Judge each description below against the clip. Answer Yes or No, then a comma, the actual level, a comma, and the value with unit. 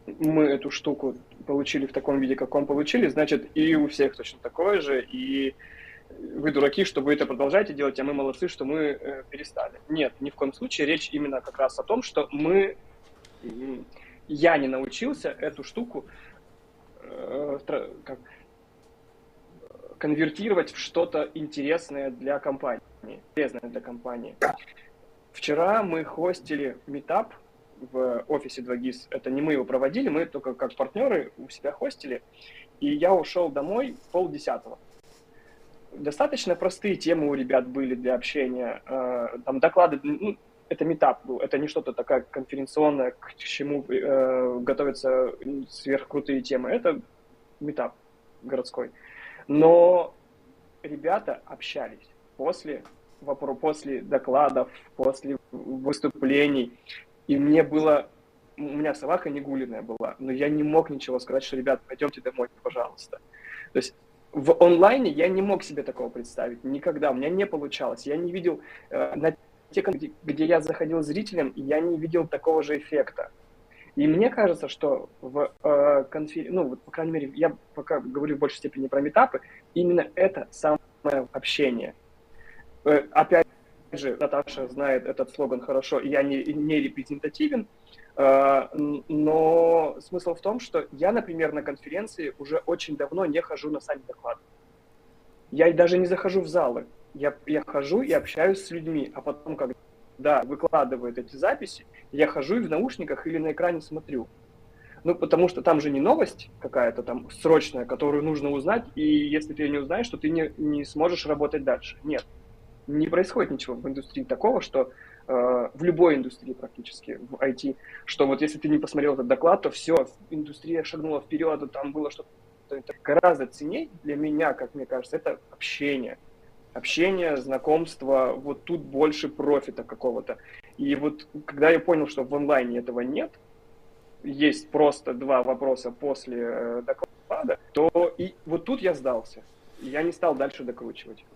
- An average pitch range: Yes, average, 3.9 semitones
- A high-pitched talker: No, medium, 150 Hz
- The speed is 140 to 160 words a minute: Yes, average, 150 wpm